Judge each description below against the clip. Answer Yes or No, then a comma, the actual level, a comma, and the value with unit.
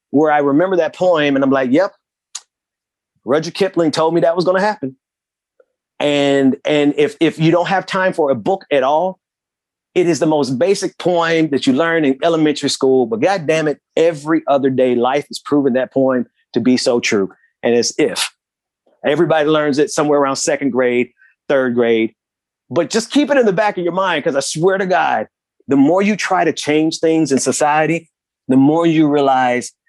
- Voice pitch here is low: No, medium, 150 Hz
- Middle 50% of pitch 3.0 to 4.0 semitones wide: No, average, 4.4 semitones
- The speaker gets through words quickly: No, average, 195 wpm